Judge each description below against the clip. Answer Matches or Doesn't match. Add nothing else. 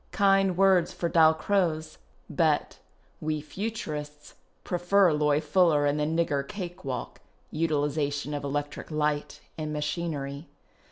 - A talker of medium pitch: Matches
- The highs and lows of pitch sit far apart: Doesn't match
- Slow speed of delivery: Matches